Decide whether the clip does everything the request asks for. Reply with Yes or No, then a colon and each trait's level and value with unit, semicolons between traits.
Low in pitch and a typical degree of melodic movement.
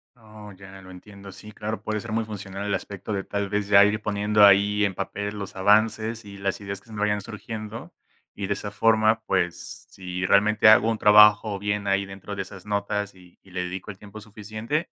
No: low, 105 Hz; narrow, 1.5 semitones